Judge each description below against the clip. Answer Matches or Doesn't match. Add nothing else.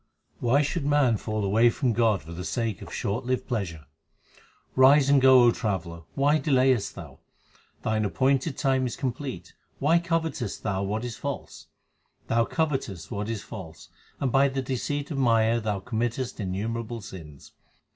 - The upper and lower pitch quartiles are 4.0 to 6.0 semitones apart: Matches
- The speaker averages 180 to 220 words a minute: Doesn't match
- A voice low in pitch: Matches